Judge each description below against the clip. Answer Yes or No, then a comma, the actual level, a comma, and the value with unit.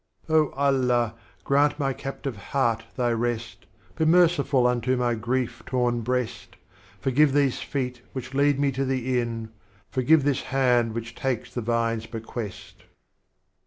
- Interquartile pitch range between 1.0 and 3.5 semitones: Yes, average, 2.7 semitones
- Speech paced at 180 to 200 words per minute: No, average, 140 wpm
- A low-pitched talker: Yes, low, 125 Hz